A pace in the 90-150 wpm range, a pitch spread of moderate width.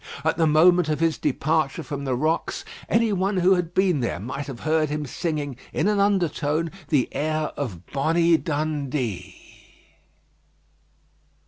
Yes: average, 145 wpm; average, 3.3 semitones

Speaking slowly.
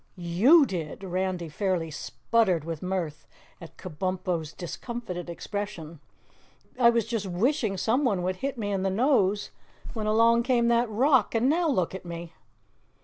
No: average, 145 wpm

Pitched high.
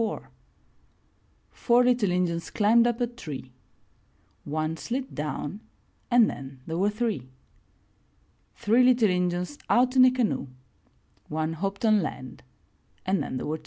Yes: high, 195 Hz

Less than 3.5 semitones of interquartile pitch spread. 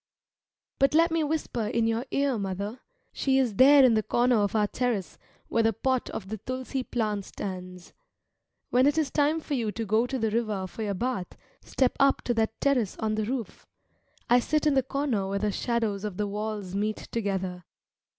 No: average, 4.2 semitones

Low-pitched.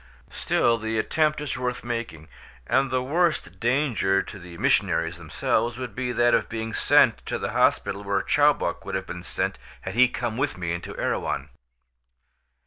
Yes: low, 115 Hz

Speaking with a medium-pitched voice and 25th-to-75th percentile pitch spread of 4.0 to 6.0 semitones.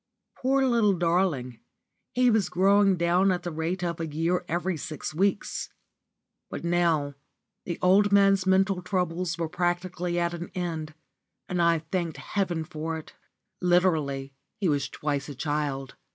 No: medium, 175 Hz; average, 2.9 semitones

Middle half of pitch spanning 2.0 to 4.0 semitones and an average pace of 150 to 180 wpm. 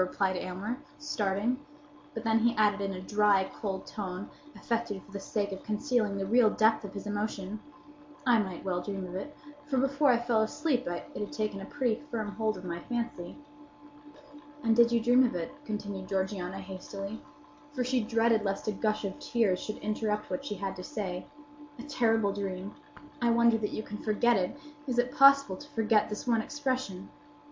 No: average, 3.4 semitones; average, 190 wpm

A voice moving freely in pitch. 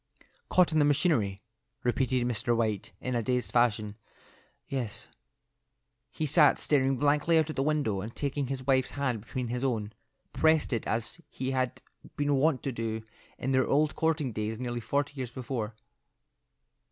No: average, 3.6 semitones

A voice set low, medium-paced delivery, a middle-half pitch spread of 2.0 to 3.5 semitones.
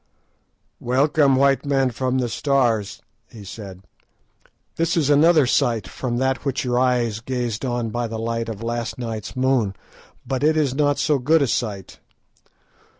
Yes: low, 125 Hz; average, 155 wpm; average, 3.1 semitones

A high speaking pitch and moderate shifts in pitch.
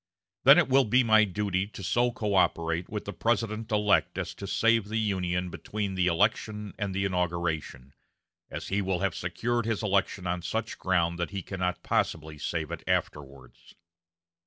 No: very low, 95 Hz; average, 3.6 semitones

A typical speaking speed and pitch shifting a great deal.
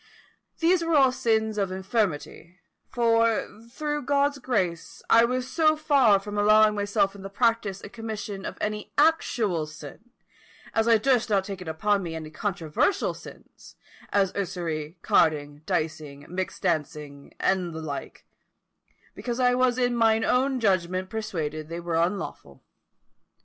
Yes: average, 145 wpm; wide, 5.9 semitones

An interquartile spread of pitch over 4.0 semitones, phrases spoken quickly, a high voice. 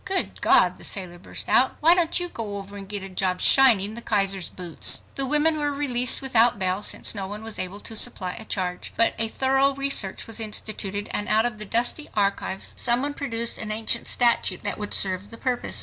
Yes: average, 4.6 semitones; fast, 215 wpm; high, 220 Hz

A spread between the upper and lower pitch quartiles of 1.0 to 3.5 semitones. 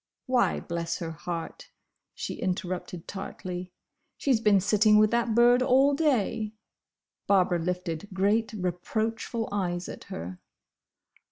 No: average, 4.2 semitones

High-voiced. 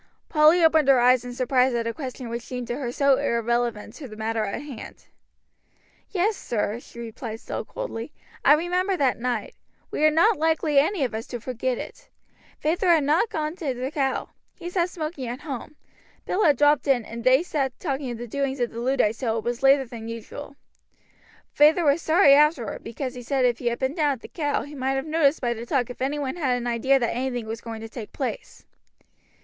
Yes: very high, 265 Hz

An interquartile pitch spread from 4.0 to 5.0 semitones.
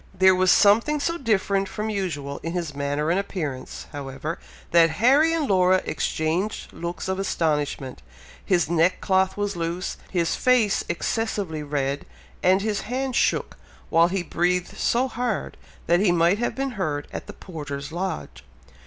Yes: average, 4.4 semitones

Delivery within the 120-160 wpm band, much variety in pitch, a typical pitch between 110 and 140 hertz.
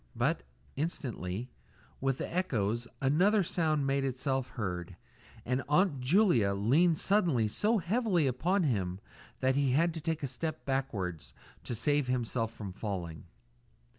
Yes: slow, 135 wpm; wide, 6.3 semitones; low, 135 Hz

